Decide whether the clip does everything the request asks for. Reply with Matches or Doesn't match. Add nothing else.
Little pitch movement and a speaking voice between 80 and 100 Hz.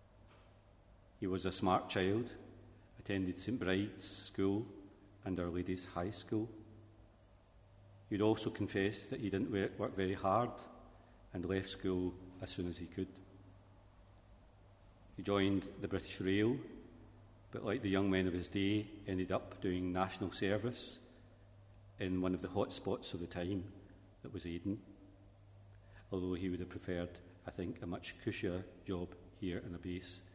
Matches